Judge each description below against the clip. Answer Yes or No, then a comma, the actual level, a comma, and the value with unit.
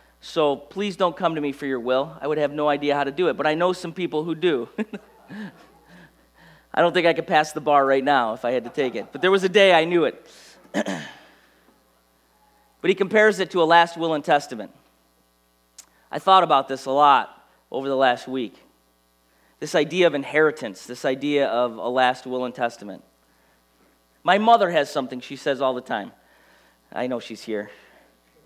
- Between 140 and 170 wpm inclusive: No, average, 200 wpm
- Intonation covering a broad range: Yes, wide, 8.0 semitones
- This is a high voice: No, medium, 140 Hz